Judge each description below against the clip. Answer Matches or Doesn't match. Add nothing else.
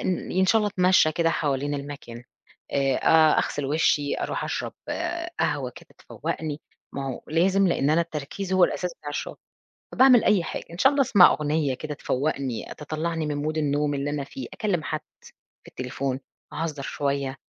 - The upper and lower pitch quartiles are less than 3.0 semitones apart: Doesn't match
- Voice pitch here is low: Doesn't match